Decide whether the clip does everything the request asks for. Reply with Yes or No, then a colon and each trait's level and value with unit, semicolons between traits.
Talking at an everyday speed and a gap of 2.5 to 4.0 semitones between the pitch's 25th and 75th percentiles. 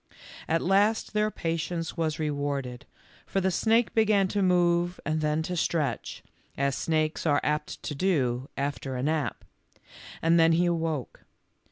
Yes: average, 150 wpm; average, 3.5 semitones